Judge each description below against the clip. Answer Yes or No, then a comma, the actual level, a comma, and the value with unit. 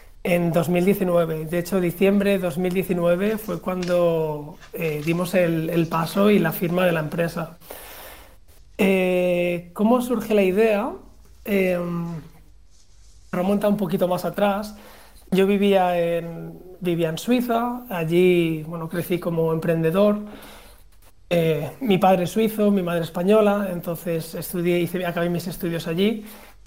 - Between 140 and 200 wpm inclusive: No, average, 130 wpm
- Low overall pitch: No, medium, 175 Hz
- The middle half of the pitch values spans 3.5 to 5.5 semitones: No, average, 2.9 semitones